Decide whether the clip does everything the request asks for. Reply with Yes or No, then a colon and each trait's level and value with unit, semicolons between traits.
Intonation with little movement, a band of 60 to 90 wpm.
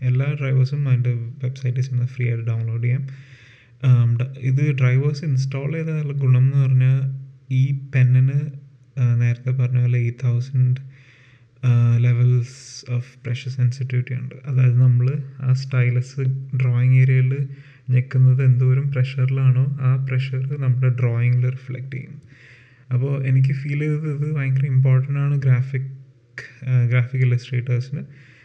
No: narrow, 1.3 semitones; average, 115 wpm